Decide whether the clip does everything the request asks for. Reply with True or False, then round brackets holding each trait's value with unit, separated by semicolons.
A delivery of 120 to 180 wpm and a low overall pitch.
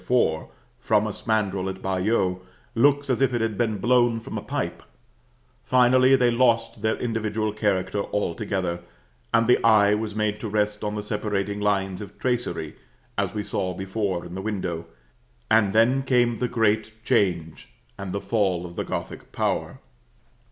True (165 wpm; 105 Hz)